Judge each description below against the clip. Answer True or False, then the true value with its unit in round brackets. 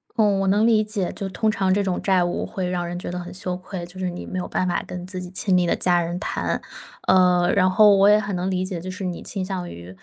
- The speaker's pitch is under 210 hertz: True (185 Hz)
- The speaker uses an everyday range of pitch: False (1.7 semitones)